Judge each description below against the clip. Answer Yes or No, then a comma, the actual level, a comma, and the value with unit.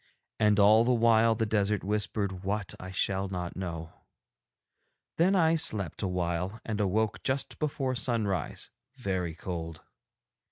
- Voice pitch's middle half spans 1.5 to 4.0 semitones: Yes, average, 3.7 semitones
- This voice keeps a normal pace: No, slow, 130 wpm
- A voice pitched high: No, low, 100 Hz